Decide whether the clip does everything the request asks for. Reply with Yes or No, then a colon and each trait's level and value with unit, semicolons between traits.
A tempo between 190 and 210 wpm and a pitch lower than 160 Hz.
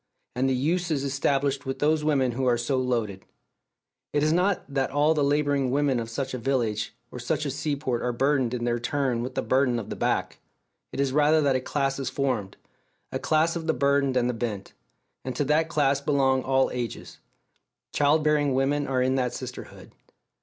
Yes: fast, 205 wpm; low, 135 Hz